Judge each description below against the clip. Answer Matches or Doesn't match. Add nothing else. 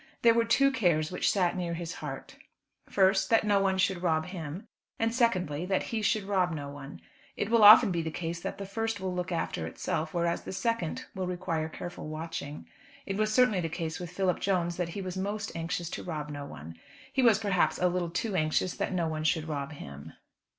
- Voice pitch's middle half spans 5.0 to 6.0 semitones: Doesn't match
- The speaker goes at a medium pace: Doesn't match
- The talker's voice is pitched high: Doesn't match